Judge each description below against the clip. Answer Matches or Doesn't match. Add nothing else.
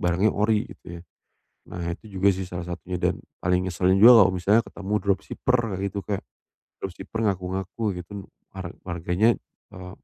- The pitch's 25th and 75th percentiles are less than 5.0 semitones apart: Matches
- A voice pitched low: Matches